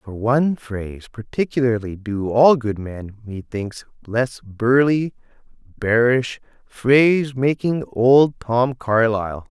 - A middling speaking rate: No, slow, 105 wpm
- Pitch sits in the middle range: No, low, 120 Hz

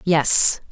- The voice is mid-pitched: Yes, medium, 160 Hz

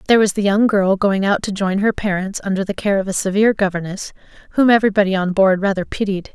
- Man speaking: No, female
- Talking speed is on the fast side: Yes, fast, 225 wpm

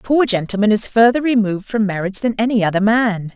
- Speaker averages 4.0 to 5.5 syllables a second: No, 6.3 syllables/s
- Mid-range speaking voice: No, high, 215 Hz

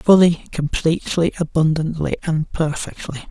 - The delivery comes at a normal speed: No, slow, 90 wpm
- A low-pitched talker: No, medium, 160 Hz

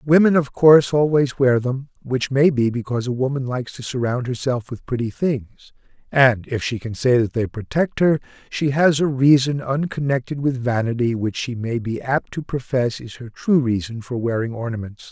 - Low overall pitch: Yes, low, 130 Hz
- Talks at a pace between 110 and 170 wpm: No, average, 195 wpm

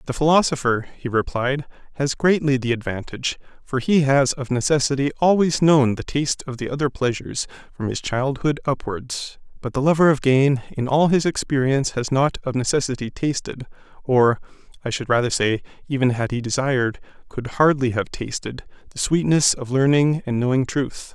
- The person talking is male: Yes, male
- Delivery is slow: No, average, 160 wpm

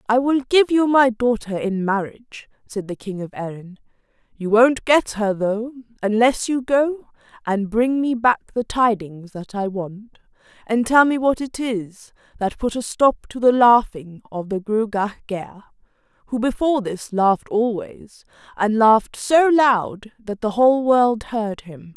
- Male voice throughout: No, female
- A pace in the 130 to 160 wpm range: No, average, 170 wpm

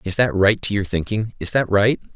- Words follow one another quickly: Yes, fast, 250 wpm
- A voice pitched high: No, low, 105 Hz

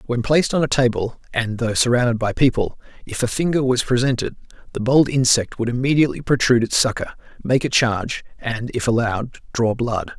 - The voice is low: Yes, low, 120 Hz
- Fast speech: No, average, 185 wpm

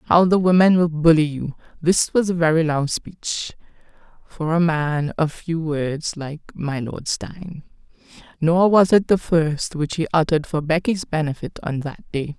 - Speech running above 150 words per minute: Yes, average, 175 wpm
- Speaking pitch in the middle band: Yes, medium, 160 Hz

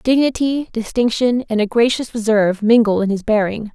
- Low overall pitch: No, high, 225 Hz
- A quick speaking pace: No, average, 160 wpm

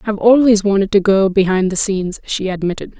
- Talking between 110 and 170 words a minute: No, average, 200 wpm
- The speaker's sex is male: No, female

